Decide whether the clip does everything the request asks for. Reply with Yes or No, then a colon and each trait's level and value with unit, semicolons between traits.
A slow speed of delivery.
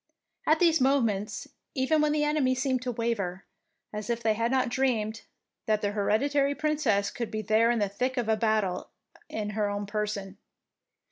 No: average, 165 wpm